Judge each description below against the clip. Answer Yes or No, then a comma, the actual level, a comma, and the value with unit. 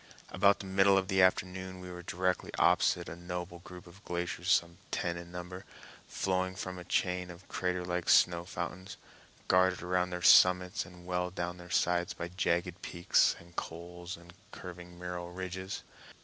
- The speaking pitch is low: Yes, very low, 90 Hz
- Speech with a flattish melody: Yes, narrow, 1.0 semitones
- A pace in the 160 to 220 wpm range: Yes, average, 170 wpm